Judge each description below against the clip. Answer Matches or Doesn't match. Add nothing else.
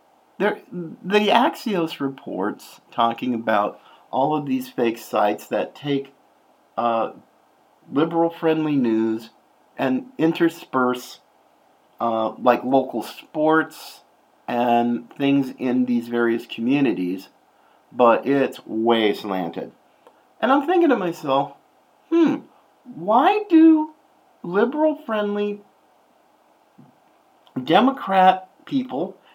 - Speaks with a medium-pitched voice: Matches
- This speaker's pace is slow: Matches